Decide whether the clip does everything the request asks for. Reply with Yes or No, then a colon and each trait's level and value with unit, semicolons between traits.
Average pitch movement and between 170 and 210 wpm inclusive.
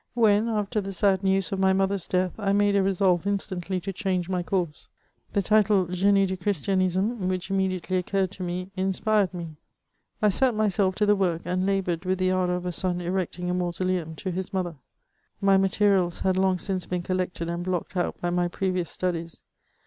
No: narrow, 1.6 semitones; average, 195 wpm